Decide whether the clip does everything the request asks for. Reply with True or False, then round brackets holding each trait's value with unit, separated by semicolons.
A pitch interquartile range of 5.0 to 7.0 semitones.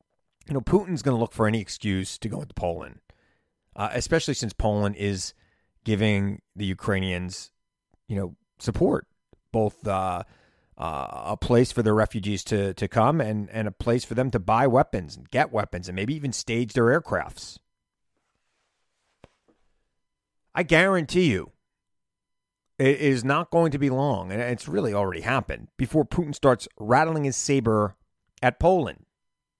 True (5.5 semitones)